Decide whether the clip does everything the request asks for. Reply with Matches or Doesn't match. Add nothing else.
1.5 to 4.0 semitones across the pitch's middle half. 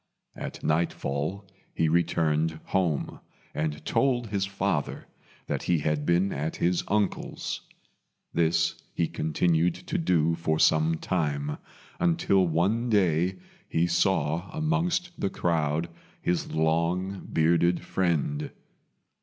Matches